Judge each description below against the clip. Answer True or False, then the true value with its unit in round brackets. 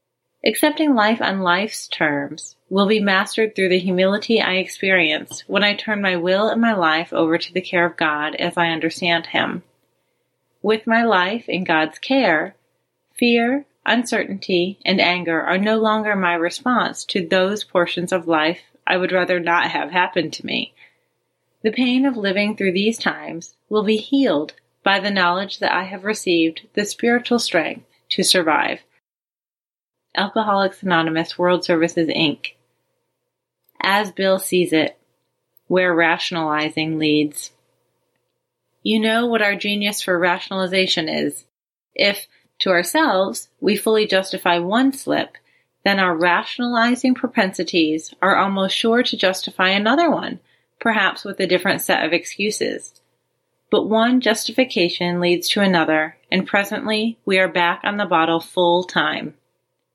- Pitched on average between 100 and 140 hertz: False (190 Hz)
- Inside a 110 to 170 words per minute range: True (145 wpm)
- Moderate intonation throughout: True (3.8 semitones)